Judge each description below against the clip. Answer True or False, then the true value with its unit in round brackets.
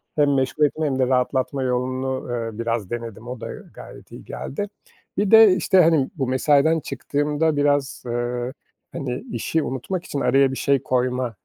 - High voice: False (130 Hz)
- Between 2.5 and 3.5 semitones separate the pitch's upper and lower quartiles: True (2.9 semitones)